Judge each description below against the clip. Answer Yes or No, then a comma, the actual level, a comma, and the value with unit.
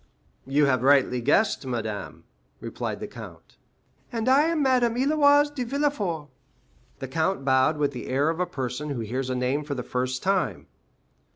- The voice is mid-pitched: Yes, medium, 145 Hz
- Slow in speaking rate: No, average, 170 wpm